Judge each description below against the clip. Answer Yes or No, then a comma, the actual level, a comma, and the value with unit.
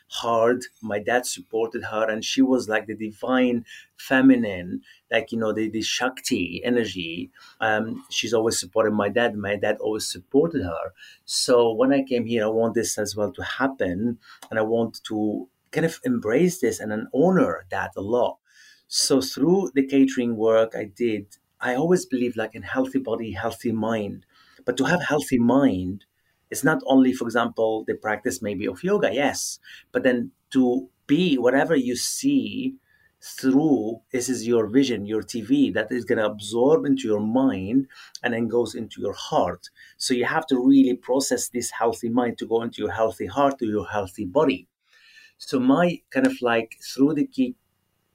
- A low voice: Yes, low, 120 Hz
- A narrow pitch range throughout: No, average, 3.5 semitones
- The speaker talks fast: No, average, 180 wpm